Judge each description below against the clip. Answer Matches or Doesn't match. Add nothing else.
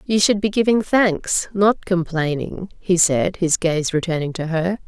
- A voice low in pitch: Doesn't match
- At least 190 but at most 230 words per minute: Doesn't match